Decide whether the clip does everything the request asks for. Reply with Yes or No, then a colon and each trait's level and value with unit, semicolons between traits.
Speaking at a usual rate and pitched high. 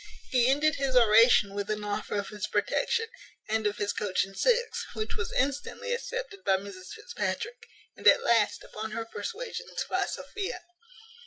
Yes: average, 165 wpm; high, 225 Hz